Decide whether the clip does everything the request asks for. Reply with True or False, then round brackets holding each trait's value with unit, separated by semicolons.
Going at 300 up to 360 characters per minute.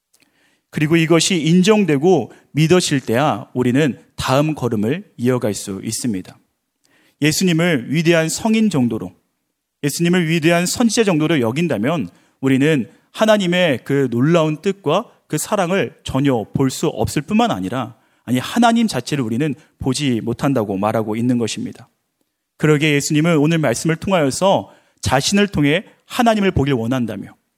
True (320 characters per minute)